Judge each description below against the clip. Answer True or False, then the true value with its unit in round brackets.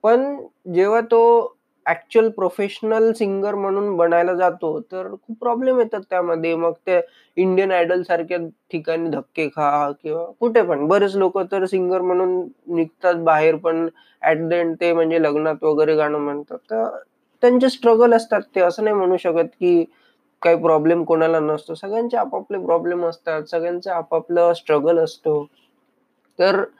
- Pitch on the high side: False (175 Hz)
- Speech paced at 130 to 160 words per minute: True (150 wpm)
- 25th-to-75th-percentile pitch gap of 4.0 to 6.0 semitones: True (4.3 semitones)